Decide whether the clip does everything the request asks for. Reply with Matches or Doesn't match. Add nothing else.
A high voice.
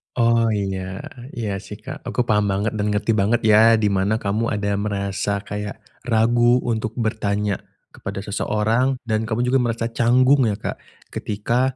Doesn't match